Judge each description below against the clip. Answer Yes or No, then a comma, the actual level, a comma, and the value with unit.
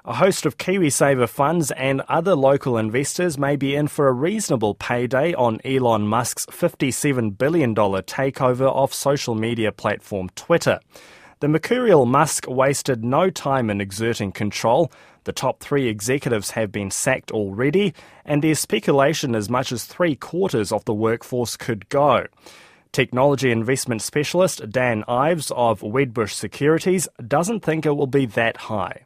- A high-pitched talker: No, low, 135 Hz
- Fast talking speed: No, average, 150 wpm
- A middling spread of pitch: Yes, average, 4.4 semitones